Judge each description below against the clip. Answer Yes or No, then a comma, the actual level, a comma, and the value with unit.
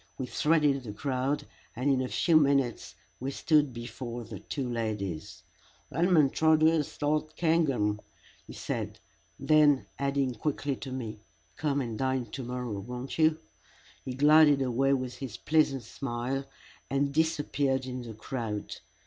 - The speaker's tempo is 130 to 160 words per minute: Yes, average, 140 wpm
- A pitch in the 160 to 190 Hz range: No, low, 135 Hz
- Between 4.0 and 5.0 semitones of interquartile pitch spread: No, average, 3.3 semitones